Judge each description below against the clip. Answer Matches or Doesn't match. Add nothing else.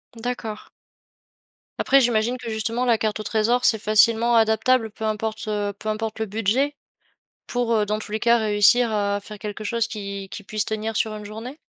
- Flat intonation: Matches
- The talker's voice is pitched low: Doesn't match